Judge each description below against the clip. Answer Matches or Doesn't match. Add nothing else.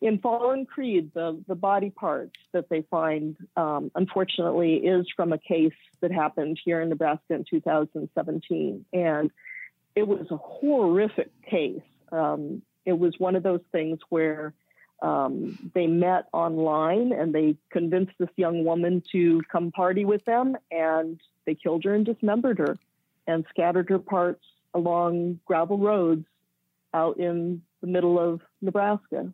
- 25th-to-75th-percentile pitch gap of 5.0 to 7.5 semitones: Doesn't match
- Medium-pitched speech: Matches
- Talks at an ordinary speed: Matches